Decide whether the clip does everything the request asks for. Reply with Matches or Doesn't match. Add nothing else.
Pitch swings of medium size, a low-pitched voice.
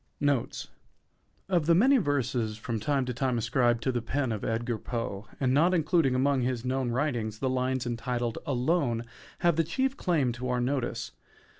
Matches